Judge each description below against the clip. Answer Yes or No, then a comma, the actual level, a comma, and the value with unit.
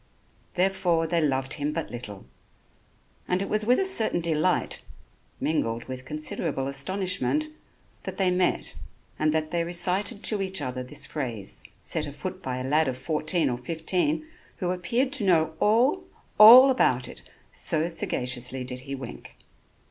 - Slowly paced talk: No, average, 155 wpm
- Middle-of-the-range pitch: Yes, medium, 165 Hz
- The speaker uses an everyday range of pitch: No, wide, 6.5 semitones